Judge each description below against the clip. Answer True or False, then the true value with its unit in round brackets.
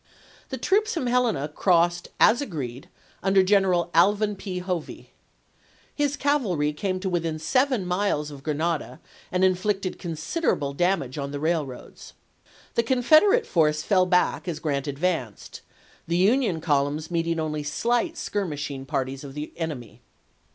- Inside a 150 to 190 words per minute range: False (140 wpm)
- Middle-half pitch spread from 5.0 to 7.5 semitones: True (5.4 semitones)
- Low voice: False (175 Hz)